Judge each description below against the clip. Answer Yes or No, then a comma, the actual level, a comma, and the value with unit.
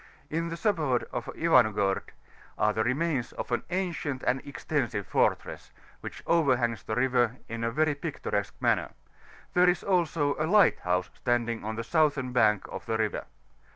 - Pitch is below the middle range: Yes, low, 130 Hz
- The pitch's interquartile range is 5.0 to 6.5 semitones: Yes, wide, 5.6 semitones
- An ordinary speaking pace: Yes, average, 155 wpm